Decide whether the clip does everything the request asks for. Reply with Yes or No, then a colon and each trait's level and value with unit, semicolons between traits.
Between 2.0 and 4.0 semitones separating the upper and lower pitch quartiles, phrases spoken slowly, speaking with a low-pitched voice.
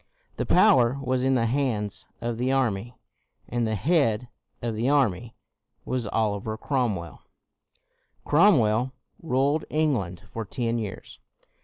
Yes: average, 3.6 semitones; slow, 125 wpm; low, 120 Hz